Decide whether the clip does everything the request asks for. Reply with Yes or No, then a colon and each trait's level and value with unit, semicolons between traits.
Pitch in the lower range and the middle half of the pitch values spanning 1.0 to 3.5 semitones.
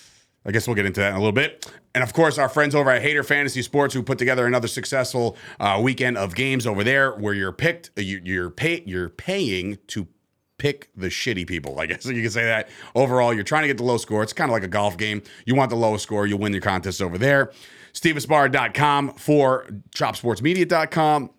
No: low, 125 Hz; average, 5.3 semitones